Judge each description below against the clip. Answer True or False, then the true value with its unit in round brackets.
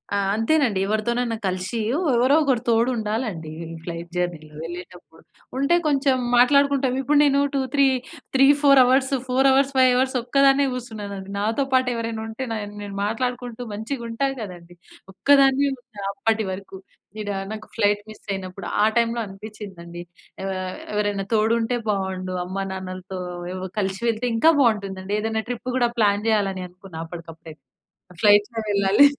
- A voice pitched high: True (220 Hz)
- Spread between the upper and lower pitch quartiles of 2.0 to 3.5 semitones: False (4.6 semitones)